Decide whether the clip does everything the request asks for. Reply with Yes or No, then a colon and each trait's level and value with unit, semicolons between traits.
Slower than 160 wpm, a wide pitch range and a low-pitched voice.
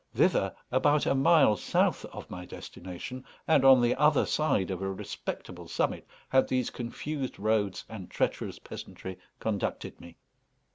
Yes: average, 145 wpm; wide, 5.8 semitones; low, 120 Hz